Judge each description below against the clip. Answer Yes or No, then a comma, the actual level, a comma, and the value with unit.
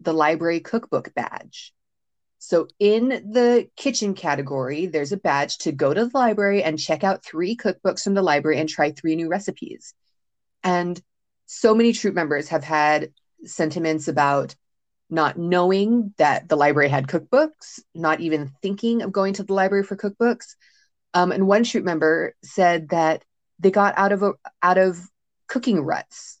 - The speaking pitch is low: No, medium, 185 Hz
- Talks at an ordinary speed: Yes, average, 165 wpm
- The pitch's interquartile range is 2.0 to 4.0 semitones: No, average, 4.7 semitones